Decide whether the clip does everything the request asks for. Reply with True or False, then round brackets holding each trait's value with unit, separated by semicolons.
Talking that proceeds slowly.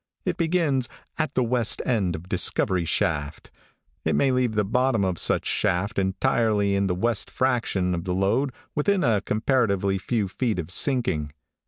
False (165 wpm)